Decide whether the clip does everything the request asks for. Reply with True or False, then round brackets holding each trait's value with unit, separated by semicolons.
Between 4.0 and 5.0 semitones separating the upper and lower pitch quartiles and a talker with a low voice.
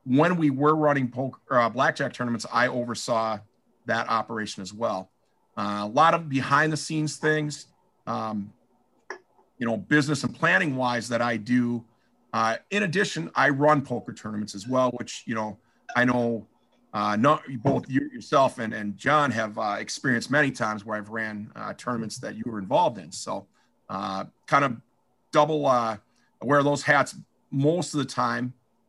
True (4.7 semitones; 125 Hz)